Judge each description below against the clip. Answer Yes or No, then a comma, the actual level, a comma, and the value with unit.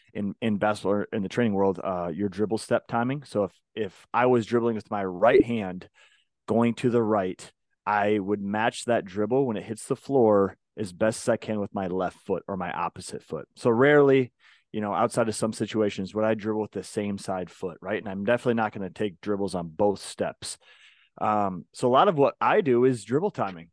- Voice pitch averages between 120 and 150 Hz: No, low, 110 Hz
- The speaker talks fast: Yes, fast, 225 wpm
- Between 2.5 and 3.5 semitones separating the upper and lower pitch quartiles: Yes, average, 2.9 semitones